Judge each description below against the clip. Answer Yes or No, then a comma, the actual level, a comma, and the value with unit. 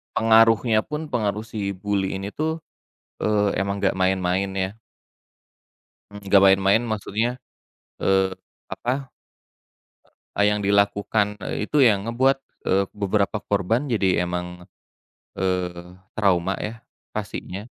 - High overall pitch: No, low, 100 Hz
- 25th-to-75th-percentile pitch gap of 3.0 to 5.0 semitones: No, narrow, 2.6 semitones